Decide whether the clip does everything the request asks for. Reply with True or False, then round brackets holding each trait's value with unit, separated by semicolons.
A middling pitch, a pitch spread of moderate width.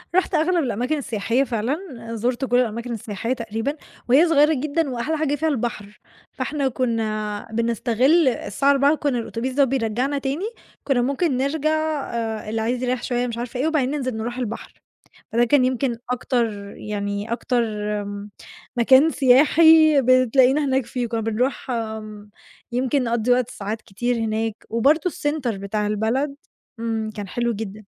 False (245 Hz; 3.6 semitones)